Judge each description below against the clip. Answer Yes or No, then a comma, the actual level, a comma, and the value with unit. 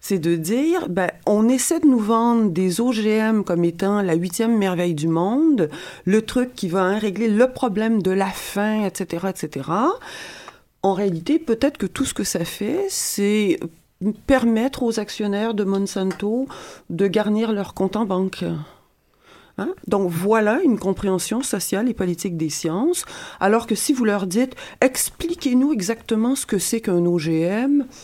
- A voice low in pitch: No, high, 210 Hz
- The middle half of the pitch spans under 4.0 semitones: No, average, 4.7 semitones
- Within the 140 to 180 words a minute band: Yes, average, 160 wpm